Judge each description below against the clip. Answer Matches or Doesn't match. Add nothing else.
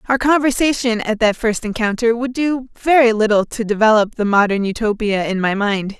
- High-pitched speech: Matches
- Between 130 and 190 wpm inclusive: Matches